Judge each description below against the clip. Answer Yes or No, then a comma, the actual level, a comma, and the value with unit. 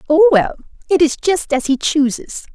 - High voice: Yes, very high, 295 Hz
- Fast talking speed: No, average, 190 wpm